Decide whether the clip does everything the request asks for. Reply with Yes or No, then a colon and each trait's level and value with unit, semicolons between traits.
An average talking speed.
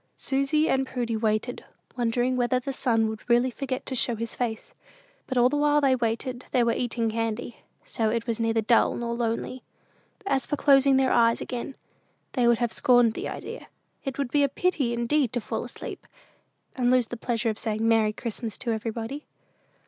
Yes: average, 190 wpm